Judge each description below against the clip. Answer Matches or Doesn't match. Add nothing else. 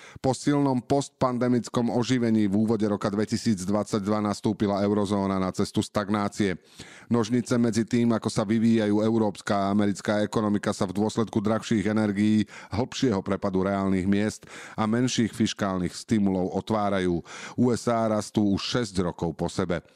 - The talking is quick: Doesn't match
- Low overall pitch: Matches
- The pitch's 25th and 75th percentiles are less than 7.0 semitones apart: Matches